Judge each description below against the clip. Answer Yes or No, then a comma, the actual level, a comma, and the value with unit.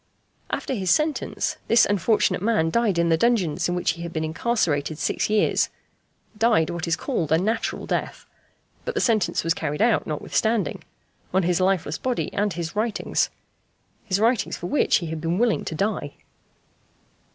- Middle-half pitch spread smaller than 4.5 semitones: No, wide, 5.5 semitones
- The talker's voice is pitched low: No, medium, 185 Hz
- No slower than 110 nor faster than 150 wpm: No, average, 170 wpm